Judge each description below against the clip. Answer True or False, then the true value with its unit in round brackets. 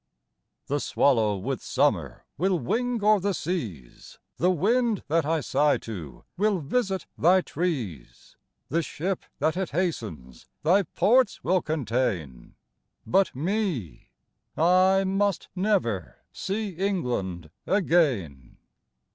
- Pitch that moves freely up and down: True (8.9 semitones)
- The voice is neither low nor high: True (165 Hz)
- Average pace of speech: False (115 wpm)